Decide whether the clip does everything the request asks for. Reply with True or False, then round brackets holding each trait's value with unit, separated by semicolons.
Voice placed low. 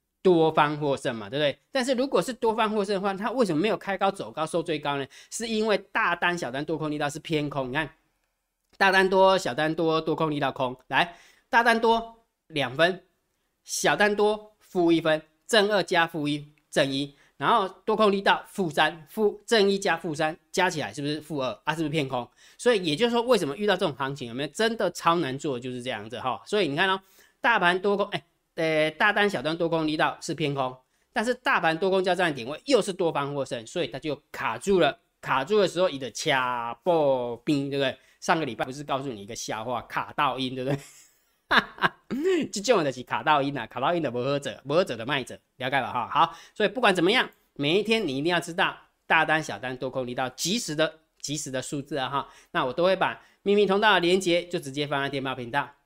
False (160 Hz)